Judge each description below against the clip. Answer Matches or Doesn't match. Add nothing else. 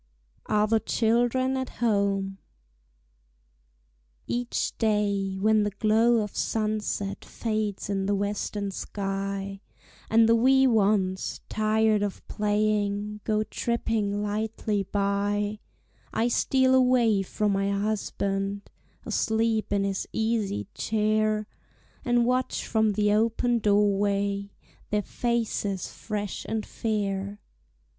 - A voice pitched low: Doesn't match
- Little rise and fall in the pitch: Matches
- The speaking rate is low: Matches